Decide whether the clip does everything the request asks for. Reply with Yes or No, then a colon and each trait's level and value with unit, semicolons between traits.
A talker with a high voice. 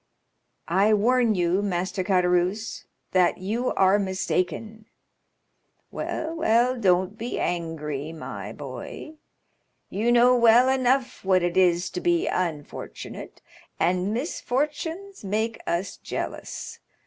Yes: high, 200 Hz